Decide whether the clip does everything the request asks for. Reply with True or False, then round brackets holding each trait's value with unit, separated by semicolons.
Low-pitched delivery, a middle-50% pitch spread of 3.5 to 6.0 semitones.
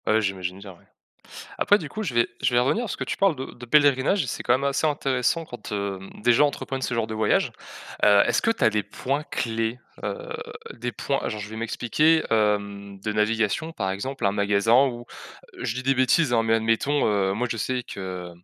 True (115 Hz; 4.8 semitones)